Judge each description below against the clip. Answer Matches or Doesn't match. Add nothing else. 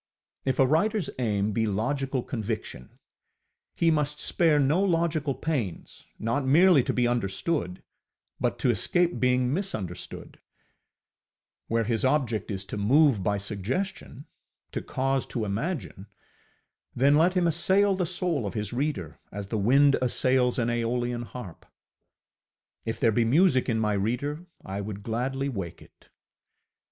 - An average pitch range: Doesn't match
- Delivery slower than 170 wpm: Matches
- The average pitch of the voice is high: Doesn't match